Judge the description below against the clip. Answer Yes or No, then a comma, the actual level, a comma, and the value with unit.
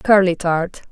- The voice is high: No, medium, 180 Hz